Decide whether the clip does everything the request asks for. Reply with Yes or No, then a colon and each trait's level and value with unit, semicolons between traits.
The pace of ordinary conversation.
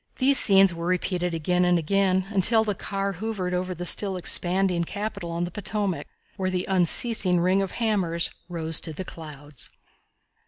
Yes: average, 165 wpm